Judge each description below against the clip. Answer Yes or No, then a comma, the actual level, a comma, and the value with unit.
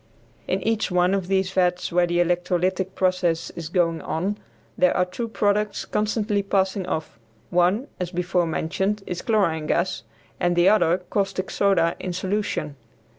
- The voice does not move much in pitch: Yes, narrow, 2.1 semitones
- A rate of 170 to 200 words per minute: No, average, 155 wpm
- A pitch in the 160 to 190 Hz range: Yes, medium, 185 Hz